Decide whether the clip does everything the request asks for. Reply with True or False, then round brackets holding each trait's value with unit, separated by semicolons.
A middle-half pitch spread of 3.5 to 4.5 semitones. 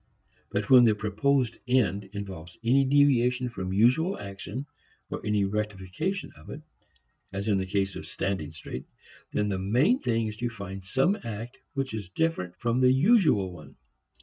False (5.0 semitones)